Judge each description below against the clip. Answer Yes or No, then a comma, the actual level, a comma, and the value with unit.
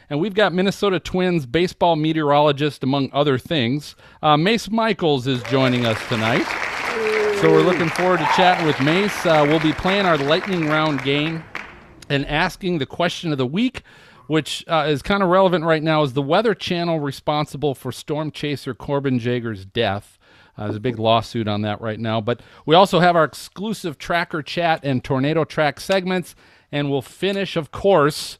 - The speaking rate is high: No, average, 180 wpm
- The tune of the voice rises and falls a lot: No, average, 4.8 semitones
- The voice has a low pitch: No, medium, 155 Hz